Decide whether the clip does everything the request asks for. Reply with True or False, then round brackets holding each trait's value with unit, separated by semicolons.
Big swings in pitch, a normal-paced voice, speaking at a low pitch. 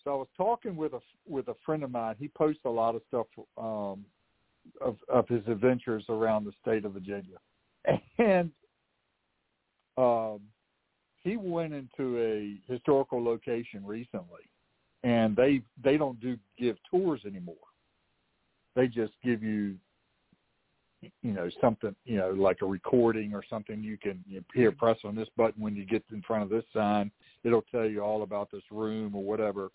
False (3.3 semitones; 170 wpm; 110 Hz)